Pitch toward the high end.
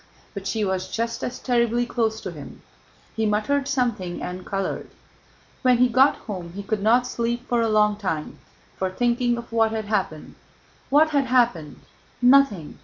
Yes: high, 225 Hz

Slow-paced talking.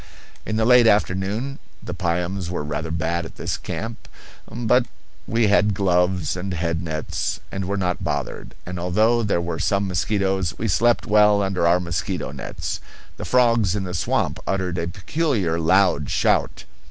No: average, 165 wpm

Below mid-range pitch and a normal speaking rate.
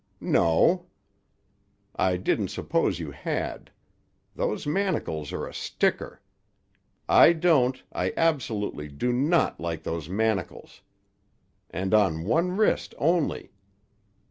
No: low, 110 Hz; slow, 100 wpm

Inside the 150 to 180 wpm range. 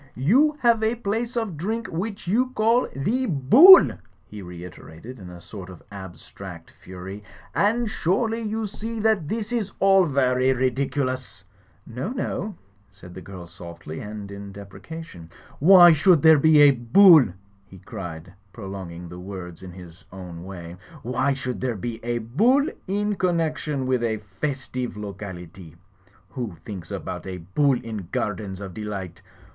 Yes: average, 155 wpm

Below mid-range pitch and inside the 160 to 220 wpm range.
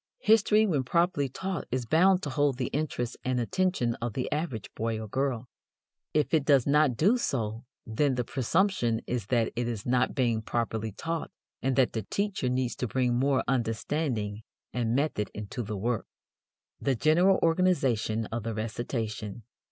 Yes: low, 125 Hz; average, 165 wpm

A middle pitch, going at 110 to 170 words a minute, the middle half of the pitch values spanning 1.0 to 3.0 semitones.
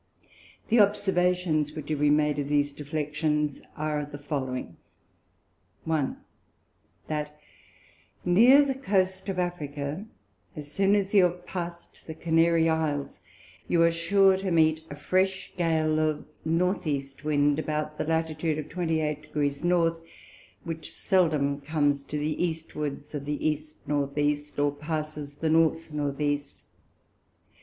Yes: medium, 155 Hz; average, 140 wpm; narrow, 2.6 semitones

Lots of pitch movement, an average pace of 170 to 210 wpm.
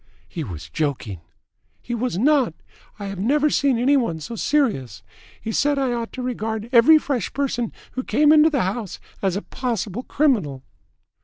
Yes: wide, 5.9 semitones; average, 175 wpm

